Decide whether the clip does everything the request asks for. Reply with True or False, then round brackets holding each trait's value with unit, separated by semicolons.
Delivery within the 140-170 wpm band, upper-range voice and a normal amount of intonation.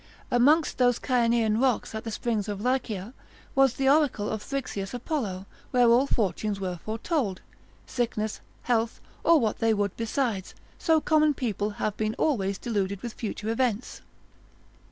True (150 wpm; 230 Hz; 3.7 semitones)